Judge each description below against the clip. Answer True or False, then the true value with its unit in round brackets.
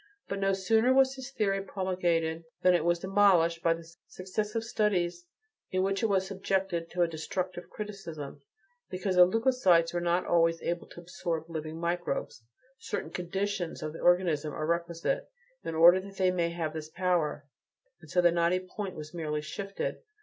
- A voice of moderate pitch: True (175 Hz)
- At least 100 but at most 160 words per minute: False (170 wpm)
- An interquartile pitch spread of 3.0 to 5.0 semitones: False (2.6 semitones)